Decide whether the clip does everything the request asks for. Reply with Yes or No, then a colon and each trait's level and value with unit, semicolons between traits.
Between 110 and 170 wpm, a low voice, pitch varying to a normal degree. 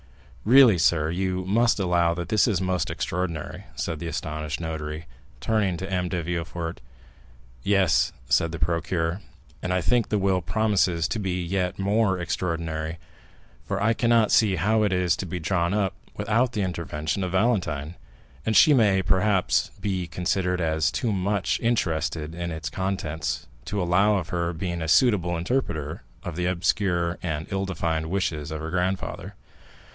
Yes: average, 160 wpm; very low, 90 Hz; average, 3.1 semitones